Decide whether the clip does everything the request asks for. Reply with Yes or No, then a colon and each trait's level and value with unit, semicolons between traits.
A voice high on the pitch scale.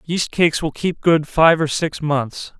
No: medium, 160 Hz